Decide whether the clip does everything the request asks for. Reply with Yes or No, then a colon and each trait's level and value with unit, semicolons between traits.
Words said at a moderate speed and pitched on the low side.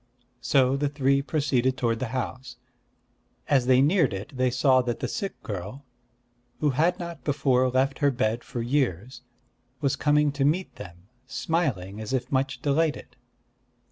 Yes: average, 155 wpm; low, 130 Hz